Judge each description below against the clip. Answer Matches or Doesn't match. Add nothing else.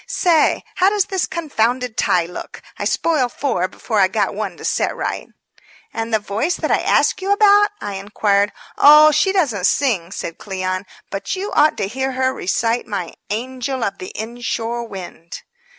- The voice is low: Doesn't match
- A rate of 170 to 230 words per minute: Matches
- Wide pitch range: Matches